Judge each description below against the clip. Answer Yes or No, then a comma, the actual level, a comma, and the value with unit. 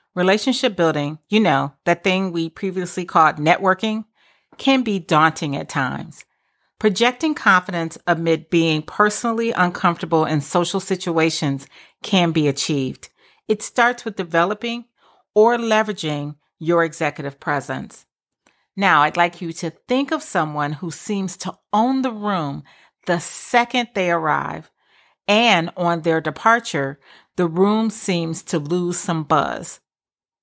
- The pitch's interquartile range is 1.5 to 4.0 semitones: No, average, 4.9 semitones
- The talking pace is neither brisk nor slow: No, slow, 130 wpm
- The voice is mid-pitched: Yes, medium, 175 Hz